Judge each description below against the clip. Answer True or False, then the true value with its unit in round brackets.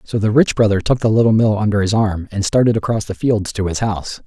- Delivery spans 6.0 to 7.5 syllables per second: True (6.1 syllables/s)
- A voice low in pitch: True (105 Hz)